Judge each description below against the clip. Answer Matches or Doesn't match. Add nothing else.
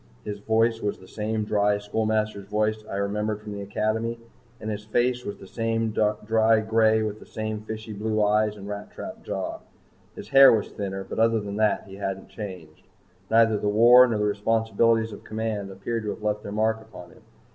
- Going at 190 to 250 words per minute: Matches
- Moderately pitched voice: Doesn't match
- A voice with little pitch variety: Matches